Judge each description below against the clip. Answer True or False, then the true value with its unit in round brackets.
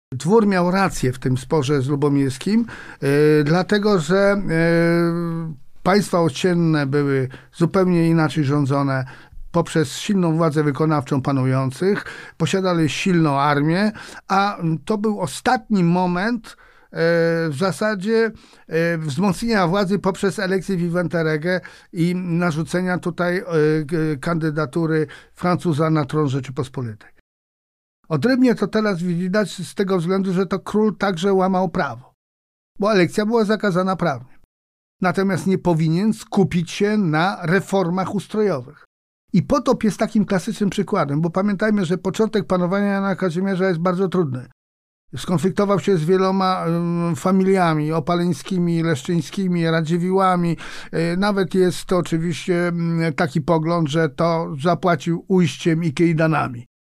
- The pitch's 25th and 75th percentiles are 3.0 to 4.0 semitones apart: True (3.3 semitones)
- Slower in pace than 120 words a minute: True (110 wpm)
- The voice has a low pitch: False (175 Hz)